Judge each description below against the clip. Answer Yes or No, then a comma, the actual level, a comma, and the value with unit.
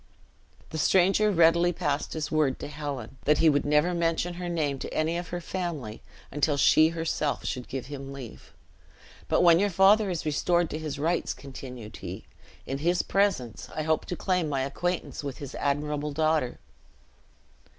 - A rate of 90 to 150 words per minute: No, average, 170 wpm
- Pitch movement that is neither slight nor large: Yes, average, 3.6 semitones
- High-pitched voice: No, medium, 155 Hz